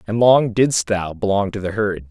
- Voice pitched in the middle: No, low, 105 Hz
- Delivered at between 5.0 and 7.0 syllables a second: No, 4.6 syllables/s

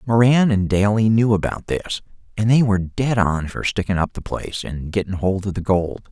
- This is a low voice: Yes, low, 100 Hz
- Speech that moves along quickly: Yes, fast, 215 wpm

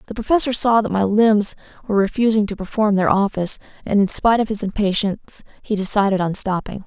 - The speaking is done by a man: No, female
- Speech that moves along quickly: No, average, 190 wpm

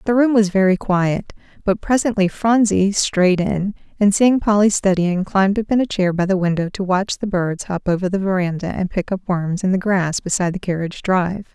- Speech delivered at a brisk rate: Yes, fast, 215 wpm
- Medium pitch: No, high, 195 Hz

